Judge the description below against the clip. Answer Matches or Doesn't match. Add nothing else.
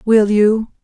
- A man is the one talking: Doesn't match